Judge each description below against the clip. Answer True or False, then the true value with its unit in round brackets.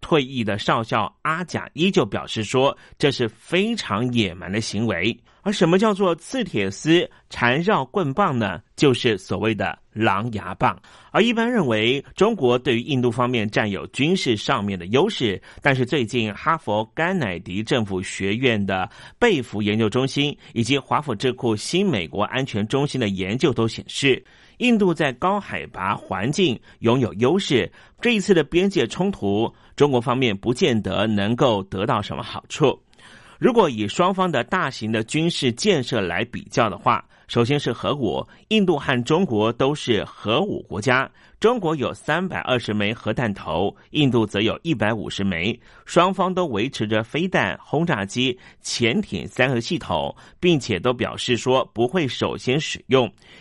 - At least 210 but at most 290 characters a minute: True (250 characters per minute)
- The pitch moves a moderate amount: False (6.7 semitones)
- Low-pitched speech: True (125 Hz)